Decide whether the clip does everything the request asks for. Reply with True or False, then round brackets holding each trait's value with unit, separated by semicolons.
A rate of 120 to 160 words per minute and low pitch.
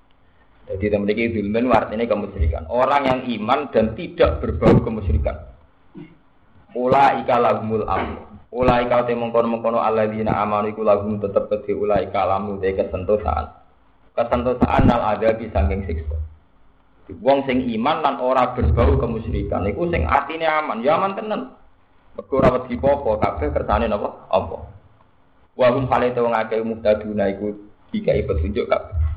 True (140 wpm; 110 Hz)